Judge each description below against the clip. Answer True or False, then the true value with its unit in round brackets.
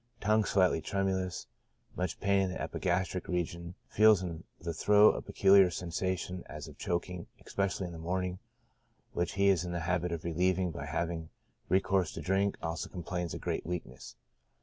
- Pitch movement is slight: True (2.0 semitones)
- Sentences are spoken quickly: False (170 wpm)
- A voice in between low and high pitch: False (90 Hz)